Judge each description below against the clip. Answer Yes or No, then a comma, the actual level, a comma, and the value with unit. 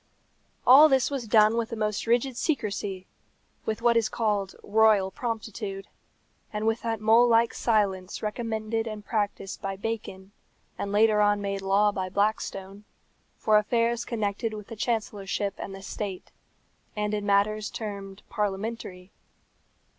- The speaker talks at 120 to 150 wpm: Yes, average, 140 wpm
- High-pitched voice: Yes, high, 210 Hz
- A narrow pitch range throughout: Yes, narrow, 2.2 semitones